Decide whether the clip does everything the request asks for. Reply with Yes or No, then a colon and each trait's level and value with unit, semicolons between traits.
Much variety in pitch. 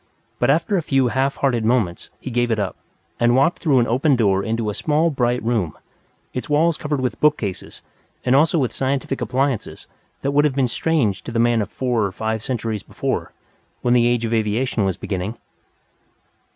No: average, 3.6 semitones